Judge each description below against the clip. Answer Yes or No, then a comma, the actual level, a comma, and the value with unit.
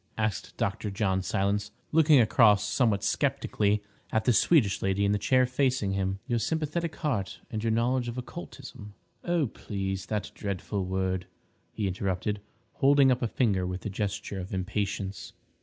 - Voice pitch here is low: Yes, low, 105 Hz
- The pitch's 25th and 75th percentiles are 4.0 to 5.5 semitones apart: Yes, average, 4.4 semitones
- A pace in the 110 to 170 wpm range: Yes, average, 155 wpm